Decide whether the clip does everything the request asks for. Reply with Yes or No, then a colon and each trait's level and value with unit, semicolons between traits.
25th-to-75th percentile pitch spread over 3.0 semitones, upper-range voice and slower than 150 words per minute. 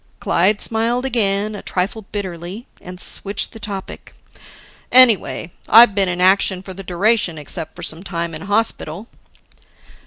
Yes: average, 3.4 semitones; high, 195 Hz; slow, 135 wpm